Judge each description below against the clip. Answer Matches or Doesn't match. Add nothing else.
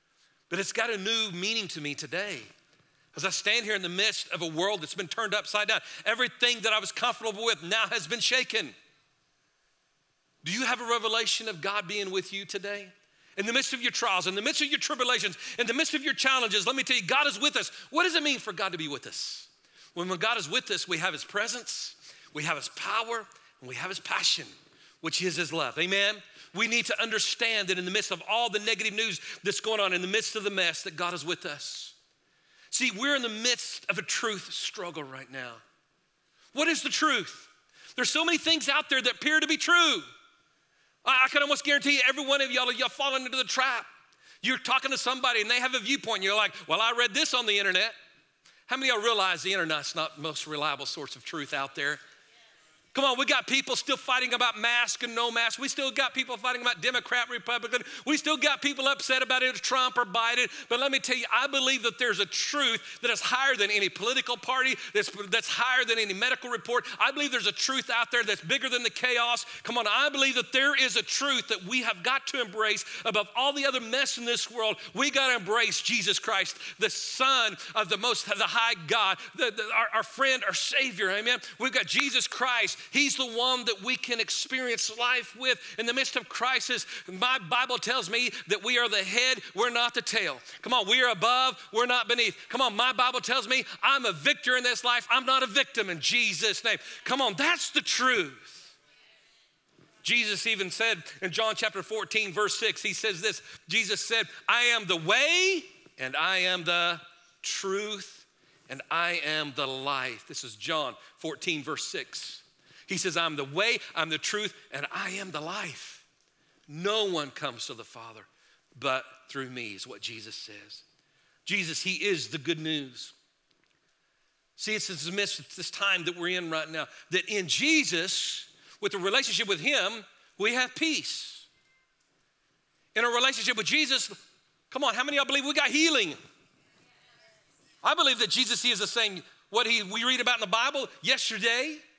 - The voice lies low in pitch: Doesn't match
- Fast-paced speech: Matches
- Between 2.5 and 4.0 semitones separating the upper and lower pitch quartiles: Doesn't match